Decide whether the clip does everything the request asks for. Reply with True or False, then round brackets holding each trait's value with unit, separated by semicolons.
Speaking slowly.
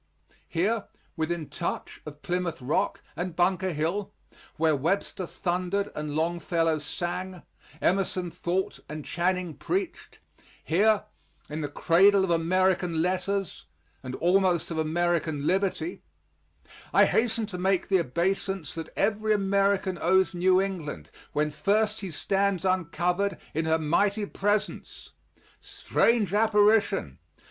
True (120 wpm)